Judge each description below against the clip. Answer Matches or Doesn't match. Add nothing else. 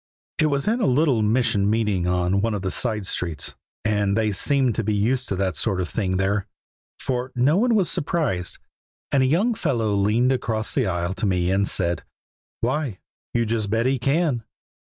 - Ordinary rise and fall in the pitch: Matches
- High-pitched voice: Doesn't match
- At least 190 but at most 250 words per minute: Matches